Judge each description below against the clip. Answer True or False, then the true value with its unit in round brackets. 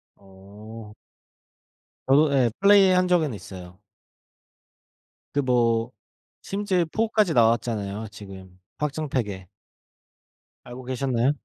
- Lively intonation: True (6.7 semitones)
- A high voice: False (120 Hz)